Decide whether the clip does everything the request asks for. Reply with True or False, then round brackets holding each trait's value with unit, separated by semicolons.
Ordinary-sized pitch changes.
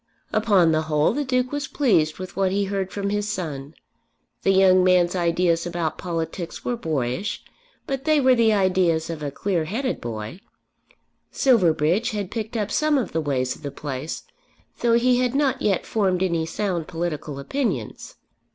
False (5.7 semitones)